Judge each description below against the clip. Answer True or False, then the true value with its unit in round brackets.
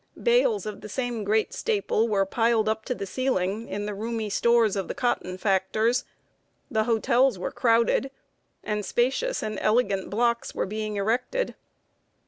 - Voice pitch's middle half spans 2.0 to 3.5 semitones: True (2.9 semitones)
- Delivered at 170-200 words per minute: False (155 wpm)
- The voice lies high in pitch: True (220 Hz)